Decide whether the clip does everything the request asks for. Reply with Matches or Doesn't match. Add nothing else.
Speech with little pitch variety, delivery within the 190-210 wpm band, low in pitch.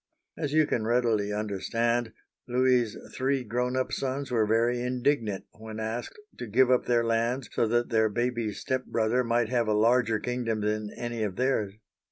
Doesn't match